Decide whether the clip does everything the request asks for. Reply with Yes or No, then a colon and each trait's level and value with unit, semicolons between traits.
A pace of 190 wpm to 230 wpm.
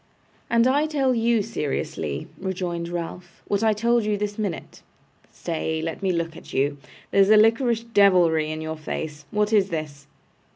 No: average, 165 wpm